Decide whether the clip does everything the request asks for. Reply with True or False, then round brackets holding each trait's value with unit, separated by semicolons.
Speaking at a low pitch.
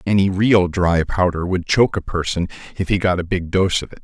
True (90 Hz)